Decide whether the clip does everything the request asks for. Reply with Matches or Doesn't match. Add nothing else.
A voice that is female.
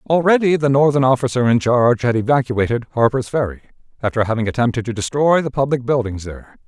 Doesn't match